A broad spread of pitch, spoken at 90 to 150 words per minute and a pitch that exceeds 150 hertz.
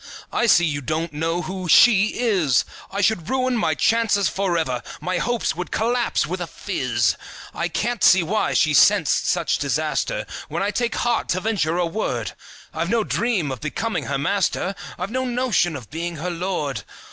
No: wide, 5.8 semitones; average, 180 wpm; medium, 185 Hz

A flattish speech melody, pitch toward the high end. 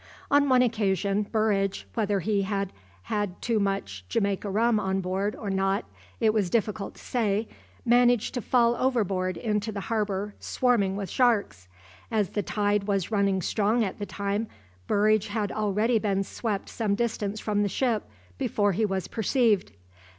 Yes: narrow, 2.2 semitones; high, 205 Hz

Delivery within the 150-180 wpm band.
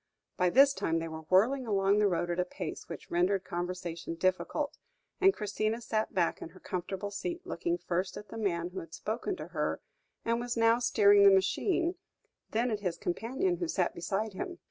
No: average, 195 wpm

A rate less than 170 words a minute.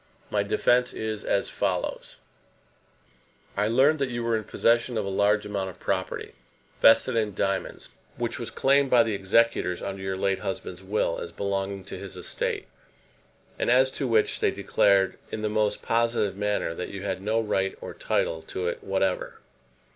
No: average, 175 wpm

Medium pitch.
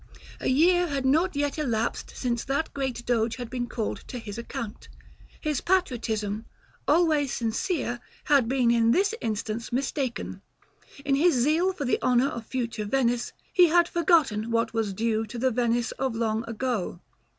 No: high, 245 Hz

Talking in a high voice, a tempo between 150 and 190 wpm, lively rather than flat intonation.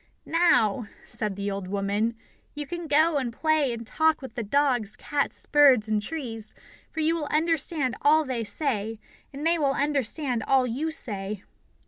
Yes: very high, 270 Hz; average, 165 wpm; wide, 5.8 semitones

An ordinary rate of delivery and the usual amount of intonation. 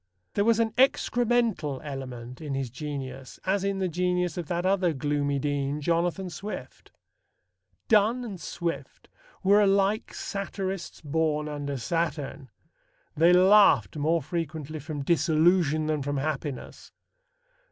No: slow, 125 wpm; average, 4.9 semitones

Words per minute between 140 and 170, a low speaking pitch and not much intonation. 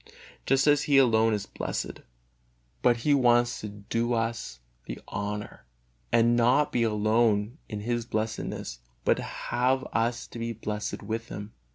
Yes: average, 150 wpm; low, 115 Hz; narrow, 2.3 semitones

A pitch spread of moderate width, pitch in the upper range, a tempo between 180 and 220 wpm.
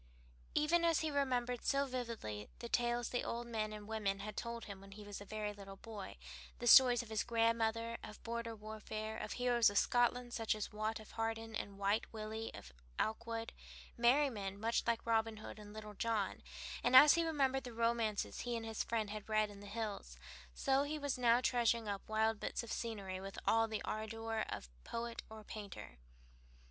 No: narrow, 2.1 semitones; high, 225 Hz; average, 200 wpm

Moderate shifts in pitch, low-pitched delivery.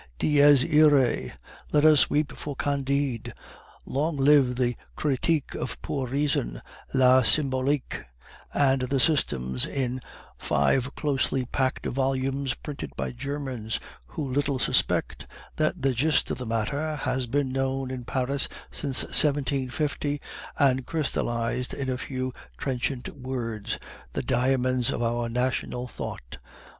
No: narrow, 2.2 semitones; low, 130 Hz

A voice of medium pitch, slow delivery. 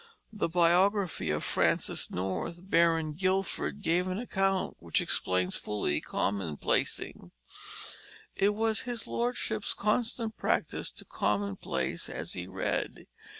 Yes: medium, 180 Hz; slow, 110 wpm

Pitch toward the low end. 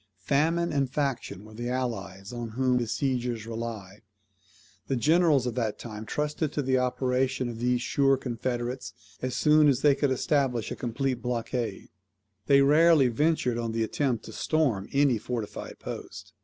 Yes: low, 125 Hz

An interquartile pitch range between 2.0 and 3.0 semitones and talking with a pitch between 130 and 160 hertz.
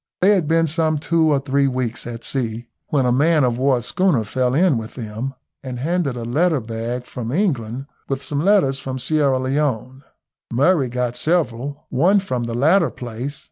No: average, 4.3 semitones; low, 135 Hz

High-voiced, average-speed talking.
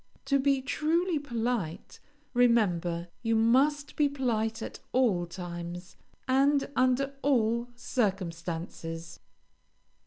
No: high, 235 Hz; slow, 95 wpm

